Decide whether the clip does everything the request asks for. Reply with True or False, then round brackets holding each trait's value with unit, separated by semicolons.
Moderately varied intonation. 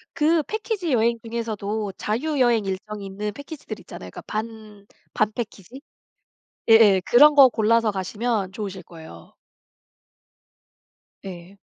True (3.4 semitones)